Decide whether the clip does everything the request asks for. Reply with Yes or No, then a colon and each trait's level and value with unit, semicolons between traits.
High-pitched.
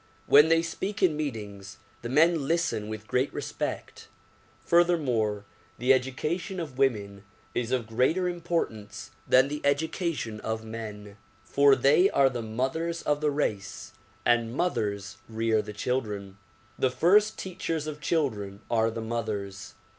No: low, 125 Hz